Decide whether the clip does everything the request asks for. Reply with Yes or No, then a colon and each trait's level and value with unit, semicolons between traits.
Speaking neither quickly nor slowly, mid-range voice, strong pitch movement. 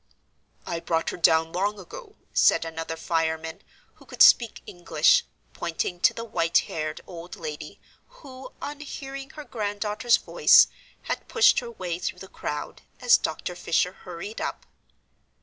Yes: average, 150 wpm; medium, 180 Hz; wide, 6.9 semitones